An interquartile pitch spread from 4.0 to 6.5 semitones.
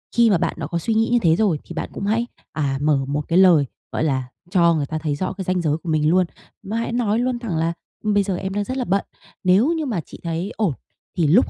Yes: wide, 5.4 semitones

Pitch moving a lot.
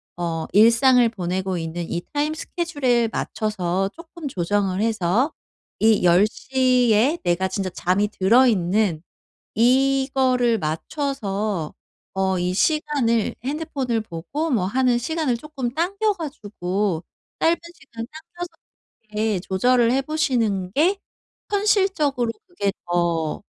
Yes: wide, 6.6 semitones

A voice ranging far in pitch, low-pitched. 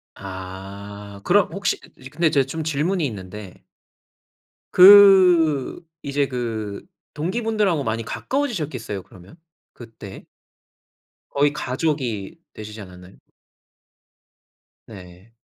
Yes: wide, 8.3 semitones; low, 130 Hz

